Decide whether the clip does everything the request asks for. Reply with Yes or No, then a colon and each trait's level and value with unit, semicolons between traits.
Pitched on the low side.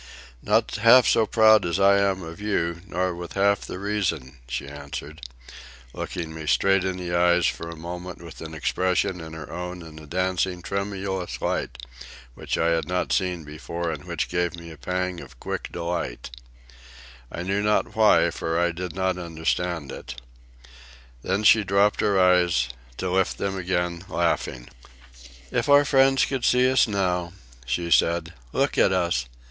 Yes: very low, 90 Hz